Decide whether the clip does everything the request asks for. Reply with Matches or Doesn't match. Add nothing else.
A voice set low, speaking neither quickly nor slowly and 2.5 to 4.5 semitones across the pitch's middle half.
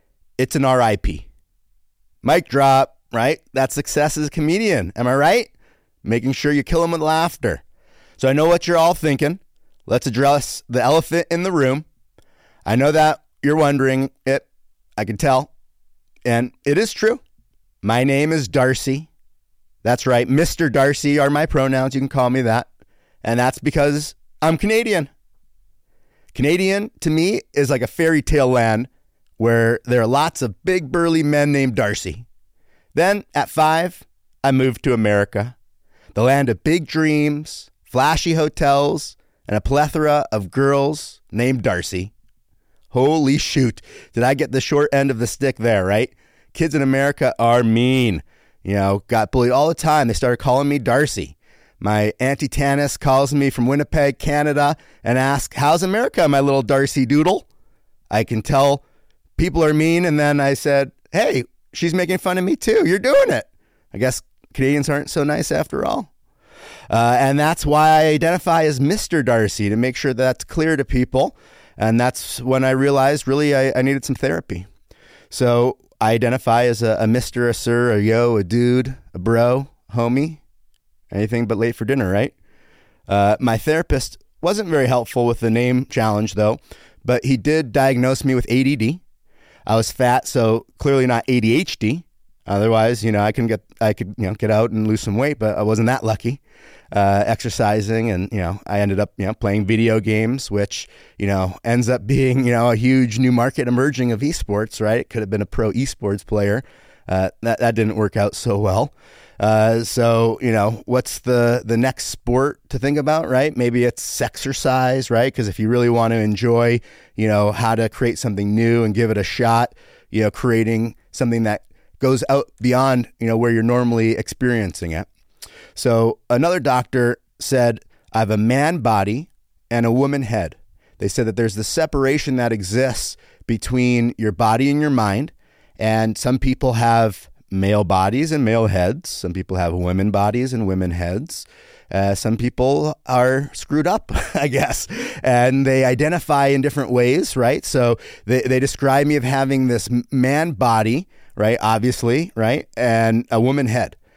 Matches